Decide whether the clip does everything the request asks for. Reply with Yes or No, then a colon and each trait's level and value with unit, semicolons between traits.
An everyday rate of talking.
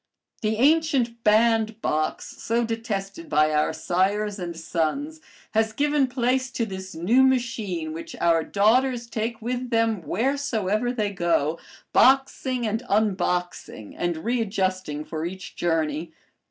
No: slow, 125 wpm